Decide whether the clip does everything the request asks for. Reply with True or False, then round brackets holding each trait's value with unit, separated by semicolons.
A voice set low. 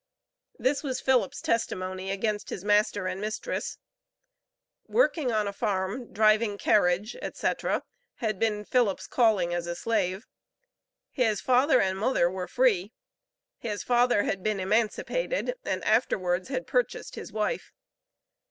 False (215 Hz)